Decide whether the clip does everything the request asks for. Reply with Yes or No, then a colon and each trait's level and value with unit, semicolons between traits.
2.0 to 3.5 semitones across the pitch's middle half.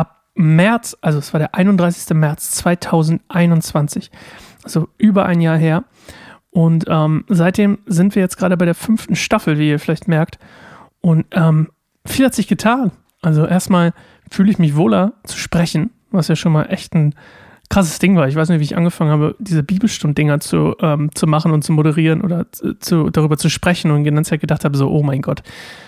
Yes: average, 3.0 semitones